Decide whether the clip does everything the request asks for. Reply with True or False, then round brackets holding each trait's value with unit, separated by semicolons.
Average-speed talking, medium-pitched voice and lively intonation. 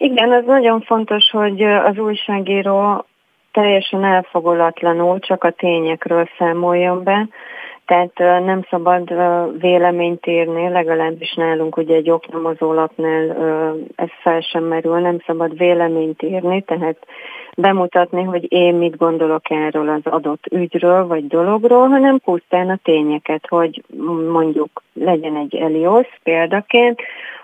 False (120 wpm; 175 Hz; 2.9 semitones)